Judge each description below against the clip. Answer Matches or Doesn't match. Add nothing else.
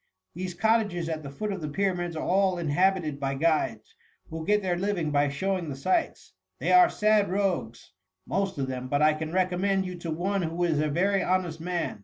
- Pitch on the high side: Doesn't match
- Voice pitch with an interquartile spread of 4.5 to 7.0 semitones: Doesn't match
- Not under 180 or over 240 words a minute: Matches